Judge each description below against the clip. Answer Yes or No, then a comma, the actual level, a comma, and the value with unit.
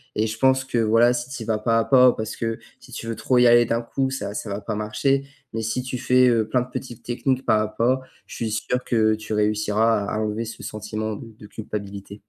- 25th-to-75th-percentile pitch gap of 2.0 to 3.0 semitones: Yes, narrow, 2.5 semitones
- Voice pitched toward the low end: Yes, low, 115 Hz